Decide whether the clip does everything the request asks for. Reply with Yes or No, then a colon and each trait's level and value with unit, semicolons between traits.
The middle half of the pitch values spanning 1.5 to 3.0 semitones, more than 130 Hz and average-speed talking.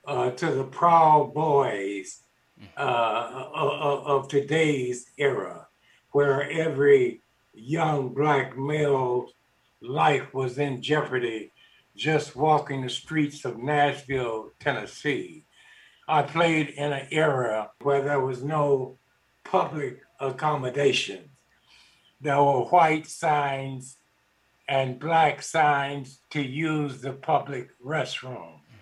No: narrow, 2.5 semitones; medium, 140 Hz; slow, 100 wpm